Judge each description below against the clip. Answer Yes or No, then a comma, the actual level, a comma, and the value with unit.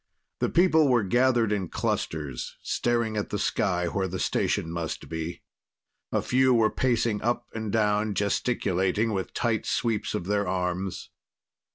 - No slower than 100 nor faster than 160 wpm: Yes, average, 150 wpm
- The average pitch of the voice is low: Yes, low, 105 Hz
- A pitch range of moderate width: Yes, average, 4.1 semitones